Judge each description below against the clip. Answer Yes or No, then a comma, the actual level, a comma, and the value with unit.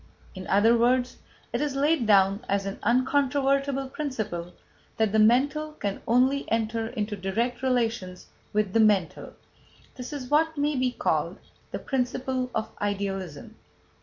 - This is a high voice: Yes, high, 235 Hz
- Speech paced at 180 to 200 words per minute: No, average, 145 wpm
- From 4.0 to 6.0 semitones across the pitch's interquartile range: Yes, average, 4.6 semitones